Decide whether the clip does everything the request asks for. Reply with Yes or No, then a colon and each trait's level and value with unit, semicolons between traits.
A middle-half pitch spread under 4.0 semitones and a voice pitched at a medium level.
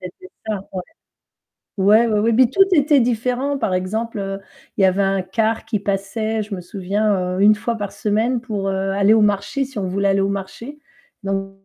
No: average, 2.8 semitones; high, 205 Hz